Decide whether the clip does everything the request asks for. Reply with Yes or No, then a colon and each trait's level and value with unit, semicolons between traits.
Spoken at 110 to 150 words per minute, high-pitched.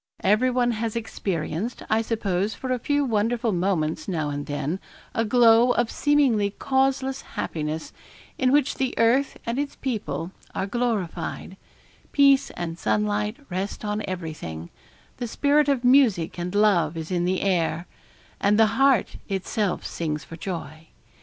Yes: average, 145 wpm; high, 210 Hz